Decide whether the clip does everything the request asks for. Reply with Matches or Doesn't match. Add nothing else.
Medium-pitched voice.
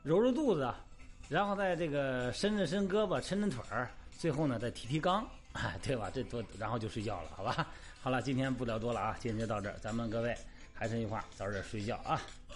Doesn't match